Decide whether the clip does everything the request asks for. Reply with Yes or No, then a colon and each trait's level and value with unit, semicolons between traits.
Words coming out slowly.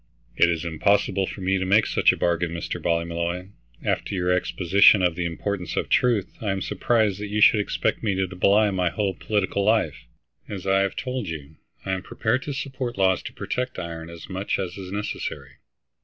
No: average, 200 wpm